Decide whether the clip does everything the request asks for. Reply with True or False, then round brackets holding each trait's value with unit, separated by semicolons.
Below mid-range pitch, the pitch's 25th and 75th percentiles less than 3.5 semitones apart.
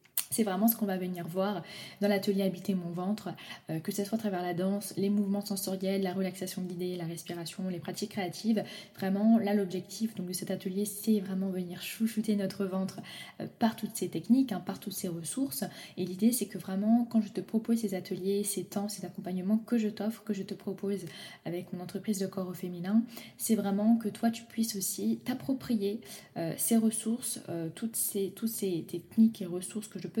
False (200 Hz; 2.8 semitones)